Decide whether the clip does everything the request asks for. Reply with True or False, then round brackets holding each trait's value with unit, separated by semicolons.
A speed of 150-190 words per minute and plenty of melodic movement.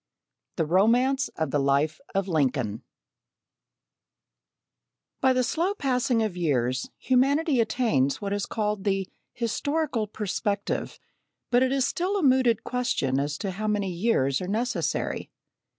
False (135 wpm; 7.9 semitones)